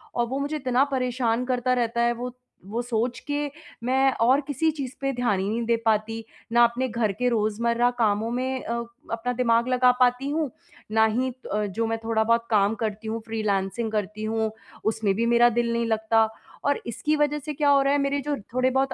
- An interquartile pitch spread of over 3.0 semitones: No, narrow, 2.6 semitones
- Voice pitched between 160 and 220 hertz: No, high, 235 Hz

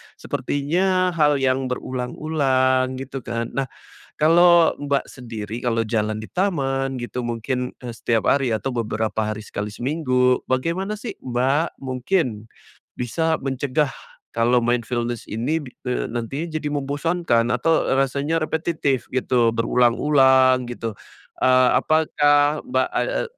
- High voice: No, low, 130 Hz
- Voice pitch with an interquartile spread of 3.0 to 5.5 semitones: Yes, average, 3.7 semitones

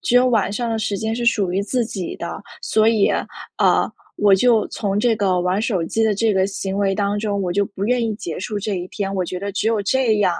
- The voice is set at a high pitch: Yes, high, 205 Hz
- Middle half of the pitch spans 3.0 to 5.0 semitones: No, narrow, 2.4 semitones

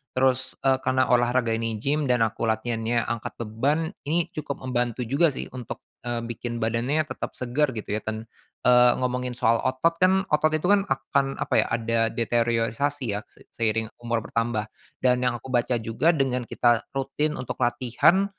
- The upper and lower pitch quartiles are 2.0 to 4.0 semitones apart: Yes, average, 2.8 semitones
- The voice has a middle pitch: No, low, 125 Hz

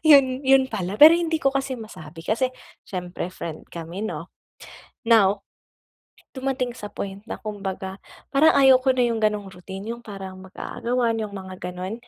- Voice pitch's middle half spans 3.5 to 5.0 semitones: No, wide, 5.4 semitones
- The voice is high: Yes, high, 215 Hz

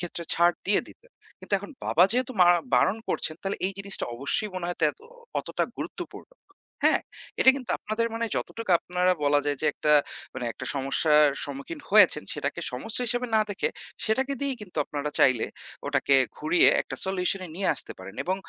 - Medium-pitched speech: Yes, medium, 180 Hz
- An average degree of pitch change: No, wide, 6.5 semitones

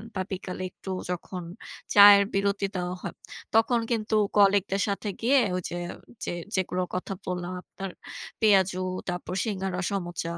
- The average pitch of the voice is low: No, high, 195 Hz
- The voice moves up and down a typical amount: No, narrow, 1.9 semitones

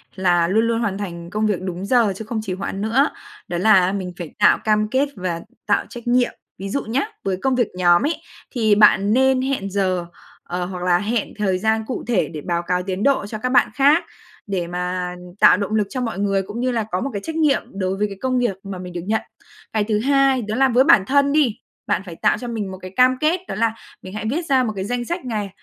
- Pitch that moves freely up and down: No, average, 4.9 semitones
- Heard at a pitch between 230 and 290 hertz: No, high, 210 Hz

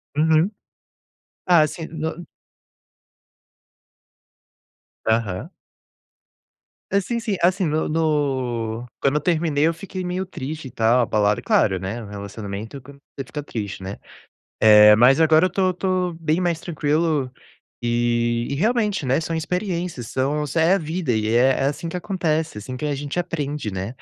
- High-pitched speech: No, medium, 150 Hz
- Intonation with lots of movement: Yes, wide, 6.2 semitones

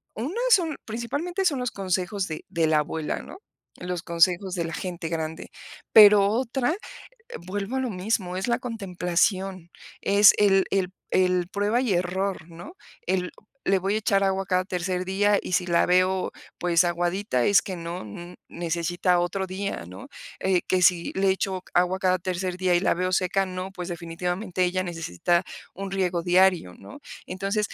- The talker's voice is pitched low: No, medium, 185 Hz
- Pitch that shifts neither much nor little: No, narrow, 2.1 semitones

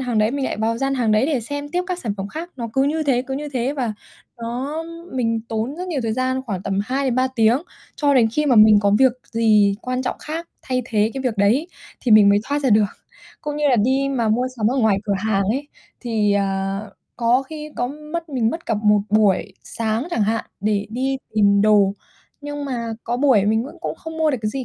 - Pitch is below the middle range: No, high, 245 Hz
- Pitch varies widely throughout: No, average, 4.3 semitones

